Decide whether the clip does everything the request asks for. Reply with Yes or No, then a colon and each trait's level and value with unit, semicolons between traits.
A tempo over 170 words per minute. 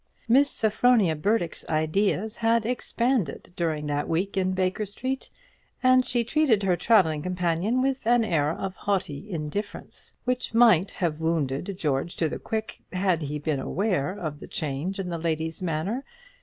No: average, 155 wpm